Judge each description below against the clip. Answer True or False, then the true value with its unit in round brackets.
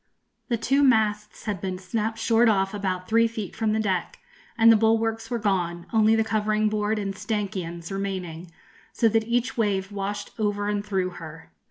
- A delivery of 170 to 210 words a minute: True (180 wpm)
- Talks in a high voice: True (210 Hz)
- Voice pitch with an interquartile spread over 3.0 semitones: False (2.6 semitones)